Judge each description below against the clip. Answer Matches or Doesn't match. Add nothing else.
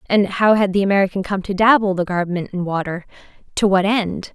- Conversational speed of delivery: Matches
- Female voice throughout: Matches